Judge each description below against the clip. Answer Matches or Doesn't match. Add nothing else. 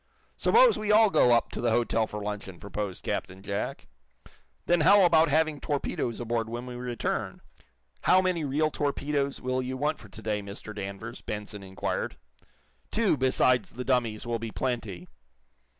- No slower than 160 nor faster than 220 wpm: Matches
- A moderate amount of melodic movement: Doesn't match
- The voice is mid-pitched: Doesn't match